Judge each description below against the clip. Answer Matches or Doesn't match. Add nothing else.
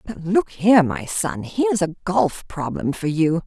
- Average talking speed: Matches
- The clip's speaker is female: Matches